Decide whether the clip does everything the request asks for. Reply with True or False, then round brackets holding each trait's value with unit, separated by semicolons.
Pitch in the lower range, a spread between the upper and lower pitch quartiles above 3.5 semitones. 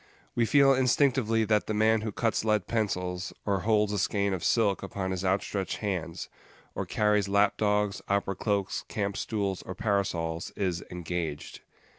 False (100 Hz; 2.5 semitones)